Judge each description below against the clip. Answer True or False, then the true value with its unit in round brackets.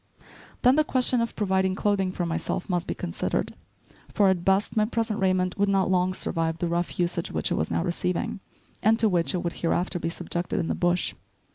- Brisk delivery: True (210 wpm)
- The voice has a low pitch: False (185 Hz)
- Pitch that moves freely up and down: False (2.8 semitones)